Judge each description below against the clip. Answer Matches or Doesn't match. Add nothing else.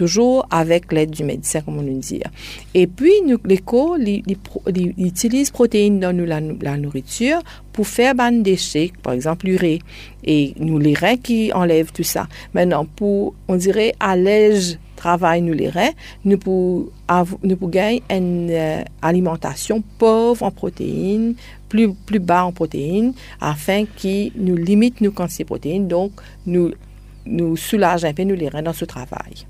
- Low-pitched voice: Doesn't match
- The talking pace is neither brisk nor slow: Matches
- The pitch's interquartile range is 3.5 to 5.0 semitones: Matches